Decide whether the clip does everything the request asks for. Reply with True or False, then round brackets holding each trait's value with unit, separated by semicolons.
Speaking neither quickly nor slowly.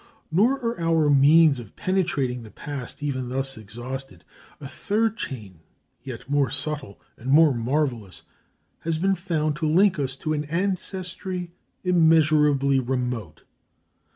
False (130 wpm)